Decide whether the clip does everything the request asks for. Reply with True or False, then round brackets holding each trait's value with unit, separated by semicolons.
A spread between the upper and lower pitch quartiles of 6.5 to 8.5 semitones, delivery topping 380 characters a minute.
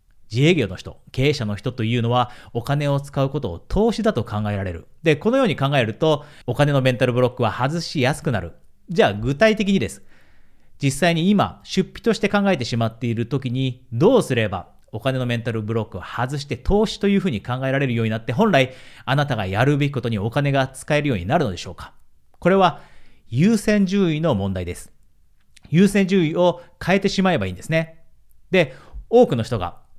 True (7.3 semitones; 390 characters per minute)